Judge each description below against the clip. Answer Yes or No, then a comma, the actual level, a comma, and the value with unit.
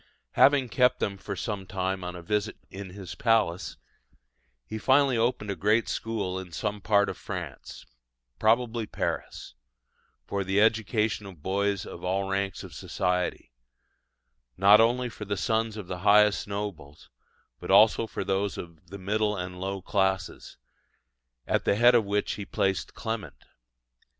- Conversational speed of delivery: Yes, average, 155 wpm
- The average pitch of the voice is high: No, low, 100 Hz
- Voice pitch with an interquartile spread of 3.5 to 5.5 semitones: No, narrow, 2.5 semitones